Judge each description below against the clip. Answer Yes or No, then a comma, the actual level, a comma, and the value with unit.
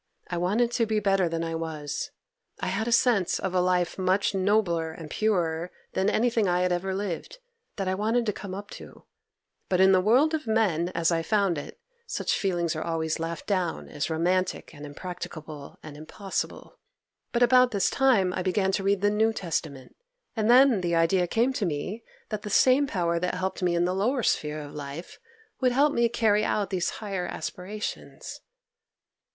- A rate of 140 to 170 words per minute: No, average, 190 wpm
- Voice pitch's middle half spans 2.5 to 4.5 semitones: Yes, average, 4.2 semitones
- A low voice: No, high, 190 Hz